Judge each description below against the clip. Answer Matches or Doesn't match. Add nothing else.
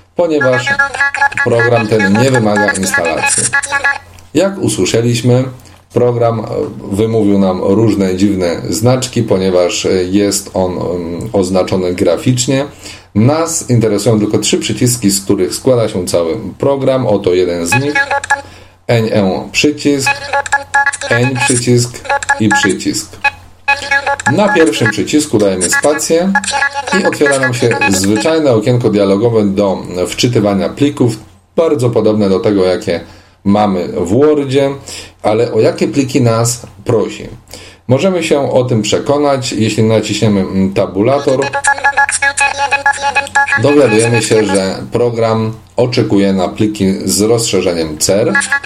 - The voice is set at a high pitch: Doesn't match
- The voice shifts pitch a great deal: Matches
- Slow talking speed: Matches